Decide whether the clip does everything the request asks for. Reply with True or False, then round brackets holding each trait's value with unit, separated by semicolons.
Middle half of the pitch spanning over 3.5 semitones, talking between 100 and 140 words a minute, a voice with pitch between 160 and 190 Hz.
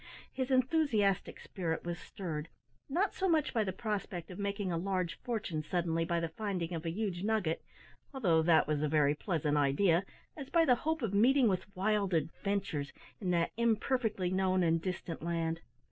False (4.7 semitones; 175 wpm; 185 Hz)